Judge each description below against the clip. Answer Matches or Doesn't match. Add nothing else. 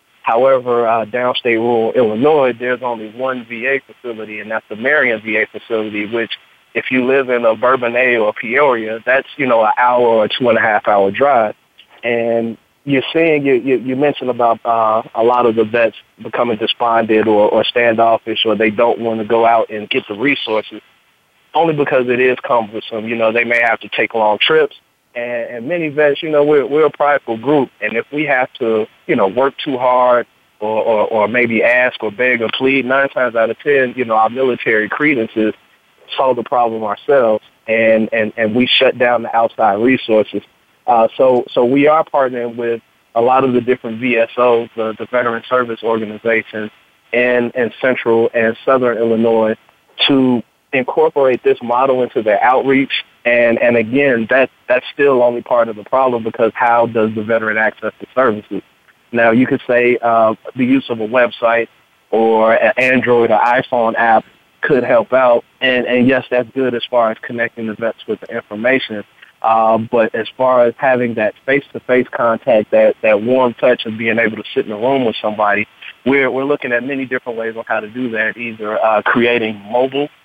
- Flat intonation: Matches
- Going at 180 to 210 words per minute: Matches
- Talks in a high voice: Doesn't match